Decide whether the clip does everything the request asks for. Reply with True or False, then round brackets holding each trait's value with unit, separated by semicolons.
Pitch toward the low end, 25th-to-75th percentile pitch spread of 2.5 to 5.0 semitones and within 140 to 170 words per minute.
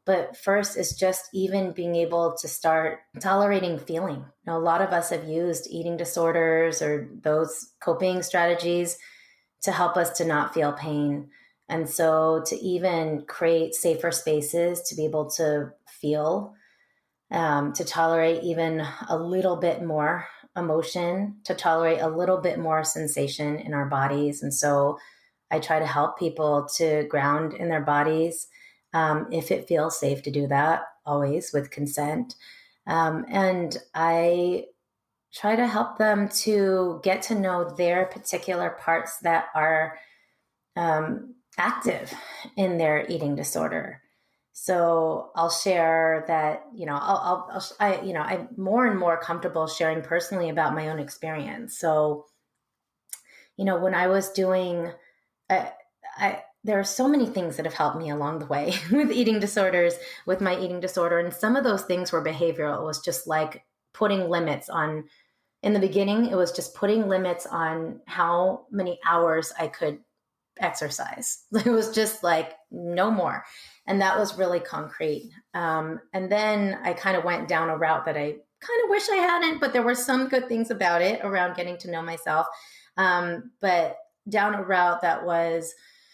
False (170 Hz; 3.1 semitones; 165 wpm)